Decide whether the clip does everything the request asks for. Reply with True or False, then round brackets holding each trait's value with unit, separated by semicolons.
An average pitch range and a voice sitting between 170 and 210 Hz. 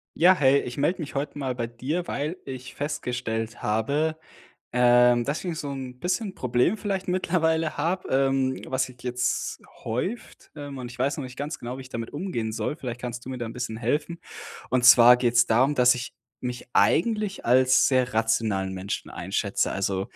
False (3.6 semitones; 130 Hz)